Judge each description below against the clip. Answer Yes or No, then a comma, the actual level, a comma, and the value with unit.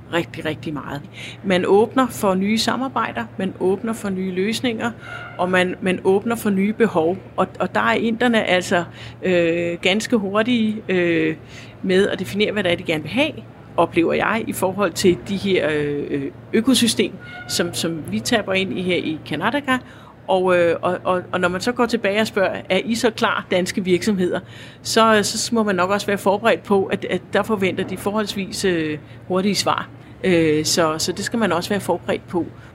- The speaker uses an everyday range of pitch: Yes, average, 4.2 semitones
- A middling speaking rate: Yes, average, 185 wpm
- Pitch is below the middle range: No, medium, 185 Hz